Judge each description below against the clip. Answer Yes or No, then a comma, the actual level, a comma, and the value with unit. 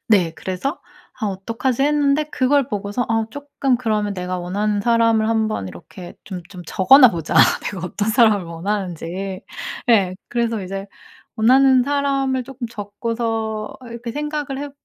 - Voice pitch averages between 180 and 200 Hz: No, high, 225 Hz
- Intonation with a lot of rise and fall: No, average, 4.8 semitones